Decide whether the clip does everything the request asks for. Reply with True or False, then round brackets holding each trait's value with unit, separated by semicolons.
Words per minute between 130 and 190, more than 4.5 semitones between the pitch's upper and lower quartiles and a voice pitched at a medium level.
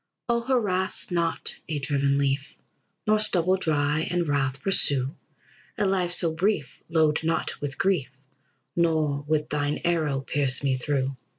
False (140 wpm; 3.9 semitones; 155 Hz)